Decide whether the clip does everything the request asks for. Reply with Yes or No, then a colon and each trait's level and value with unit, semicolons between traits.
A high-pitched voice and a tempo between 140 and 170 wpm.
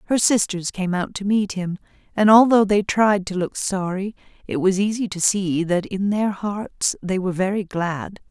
No: high, 195 Hz; average, 195 wpm